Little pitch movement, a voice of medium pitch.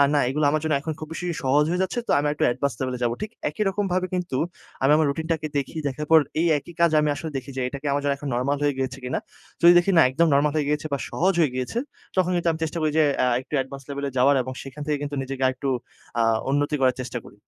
No: average, 3.2 semitones; medium, 145 Hz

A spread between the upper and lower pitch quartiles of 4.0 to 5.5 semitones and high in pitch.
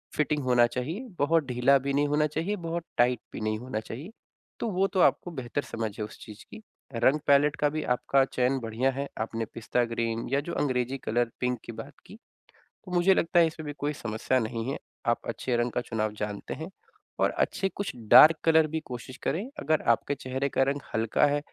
No: average, 4.5 semitones; low, 135 Hz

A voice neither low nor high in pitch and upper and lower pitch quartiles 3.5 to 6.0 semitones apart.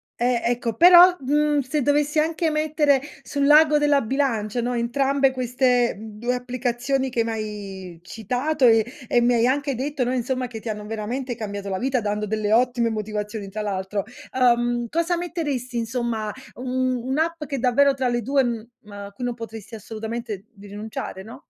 No: high, 245 Hz; average, 3.8 semitones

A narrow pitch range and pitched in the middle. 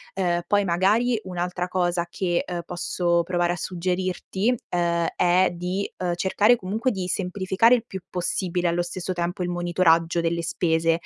Yes: narrow, 1.5 semitones; medium, 180 Hz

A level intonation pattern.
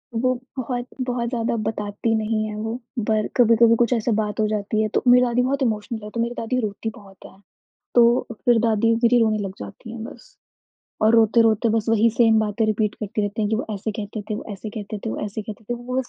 Yes: narrow, 1.9 semitones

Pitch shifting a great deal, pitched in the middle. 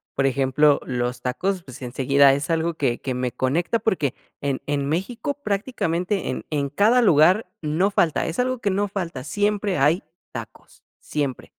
Yes: wide, 6.4 semitones; medium, 160 Hz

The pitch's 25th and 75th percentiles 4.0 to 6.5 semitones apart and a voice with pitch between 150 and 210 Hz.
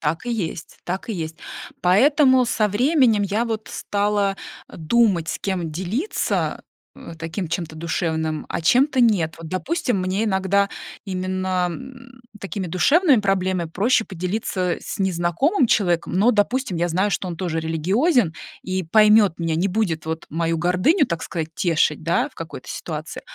Yes: average, 4.8 semitones; high, 190 Hz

